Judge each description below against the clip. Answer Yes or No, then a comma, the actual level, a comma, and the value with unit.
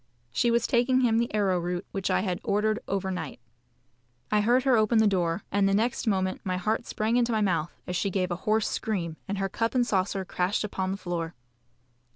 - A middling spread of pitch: Yes, average, 3.3 semitones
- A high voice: Yes, high, 200 Hz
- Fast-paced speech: Yes, fast, 210 wpm